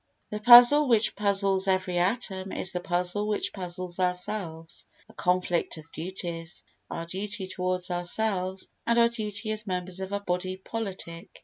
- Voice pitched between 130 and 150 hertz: No, high, 190 Hz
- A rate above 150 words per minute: No, average, 140 wpm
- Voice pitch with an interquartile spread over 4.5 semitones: No, average, 2.8 semitones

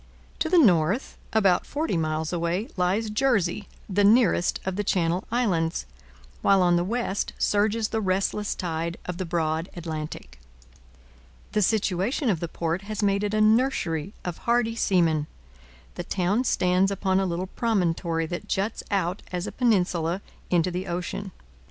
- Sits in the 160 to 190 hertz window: Yes, medium, 185 Hz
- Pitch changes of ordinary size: Yes, average, 3.6 semitones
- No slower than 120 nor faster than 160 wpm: Yes, average, 155 wpm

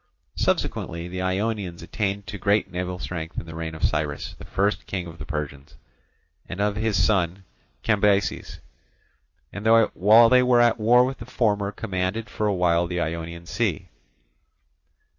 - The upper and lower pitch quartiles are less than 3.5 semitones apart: No, average, 3.9 semitones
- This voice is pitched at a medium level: No, very low, 95 Hz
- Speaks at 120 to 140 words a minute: No, average, 160 wpm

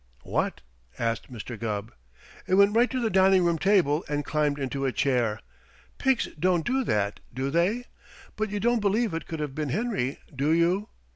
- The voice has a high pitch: No, medium, 165 Hz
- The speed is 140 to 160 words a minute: No, average, 185 wpm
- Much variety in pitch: Yes, wide, 7.3 semitones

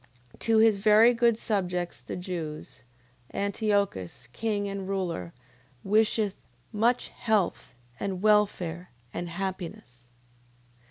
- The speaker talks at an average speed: No, slow, 100 wpm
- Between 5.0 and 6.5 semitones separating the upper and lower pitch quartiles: No, average, 3.5 semitones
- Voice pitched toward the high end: Yes, high, 195 Hz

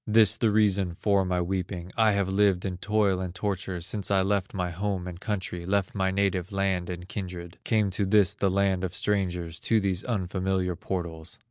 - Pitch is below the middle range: Yes, very low, 95 Hz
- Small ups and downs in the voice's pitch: Yes, narrow, 2.0 semitones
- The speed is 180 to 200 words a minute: Yes, average, 195 wpm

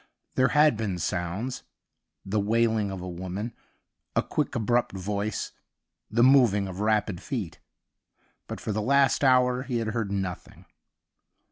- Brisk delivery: No, average, 145 wpm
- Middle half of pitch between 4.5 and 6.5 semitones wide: No, average, 4.1 semitones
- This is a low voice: Yes, low, 110 Hz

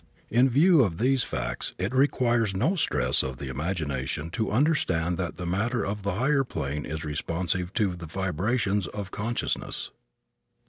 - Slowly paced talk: No, average, 155 wpm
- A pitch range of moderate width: No, wide, 6.6 semitones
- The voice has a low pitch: Yes, very low, 95 Hz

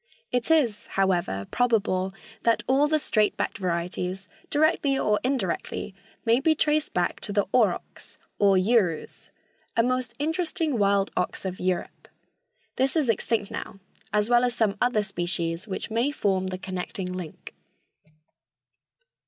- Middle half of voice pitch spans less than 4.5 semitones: No, average, 5.2 semitones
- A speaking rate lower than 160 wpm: Yes, average, 140 wpm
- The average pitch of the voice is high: Yes, high, 210 Hz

